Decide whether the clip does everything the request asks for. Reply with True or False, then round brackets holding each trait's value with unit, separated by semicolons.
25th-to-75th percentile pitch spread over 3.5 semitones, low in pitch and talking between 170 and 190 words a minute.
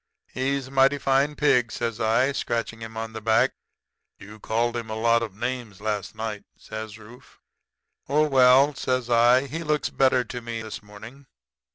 False (3.1 semitones; 120 Hz; 175 wpm)